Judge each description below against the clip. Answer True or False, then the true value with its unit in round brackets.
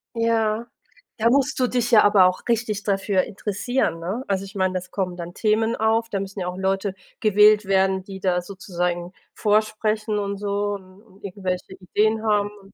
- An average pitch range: False (2.3 semitones)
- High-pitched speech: True (200 Hz)